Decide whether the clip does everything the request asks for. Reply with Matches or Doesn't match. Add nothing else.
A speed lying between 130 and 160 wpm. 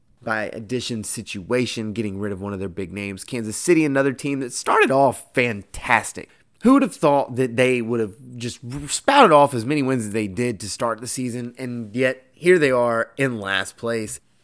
Doesn't match